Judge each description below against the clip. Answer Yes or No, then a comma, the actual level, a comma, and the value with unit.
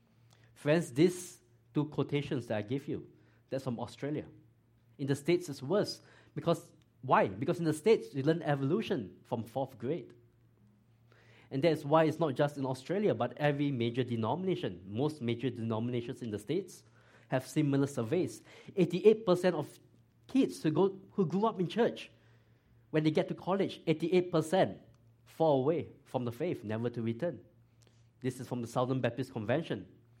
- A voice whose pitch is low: Yes, low, 130 Hz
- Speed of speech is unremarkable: Yes, average, 160 wpm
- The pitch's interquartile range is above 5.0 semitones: Yes, wide, 5.5 semitones